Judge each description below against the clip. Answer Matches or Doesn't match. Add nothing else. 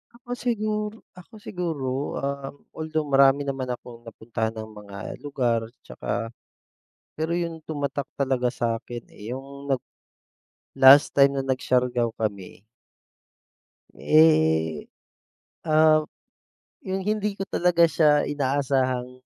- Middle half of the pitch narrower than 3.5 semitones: Doesn't match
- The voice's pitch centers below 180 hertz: Matches